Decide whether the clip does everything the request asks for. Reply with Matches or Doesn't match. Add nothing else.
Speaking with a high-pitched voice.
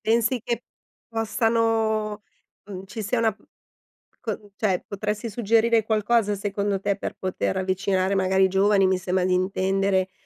Matches